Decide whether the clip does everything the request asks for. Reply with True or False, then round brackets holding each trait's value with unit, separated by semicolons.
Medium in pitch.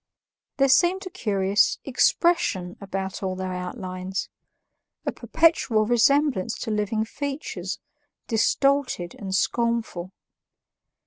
False (215 Hz)